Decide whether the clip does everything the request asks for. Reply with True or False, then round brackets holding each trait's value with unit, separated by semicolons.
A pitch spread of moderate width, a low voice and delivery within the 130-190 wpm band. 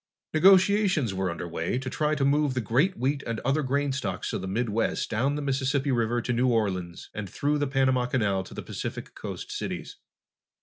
False (4.7 semitones; 130 Hz; 200 wpm)